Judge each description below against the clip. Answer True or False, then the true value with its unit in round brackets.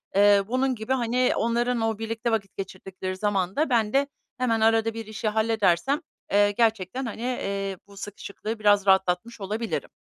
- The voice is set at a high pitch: True (220 Hz)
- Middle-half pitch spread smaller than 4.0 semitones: True (2.9 semitones)